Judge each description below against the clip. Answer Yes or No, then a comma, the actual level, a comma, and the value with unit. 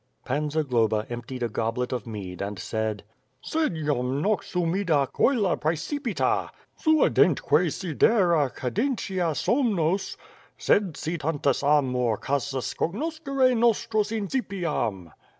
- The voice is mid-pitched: Yes, medium, 155 Hz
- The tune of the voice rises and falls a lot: Yes, wide, 8.5 semitones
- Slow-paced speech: Yes, slow, 105 wpm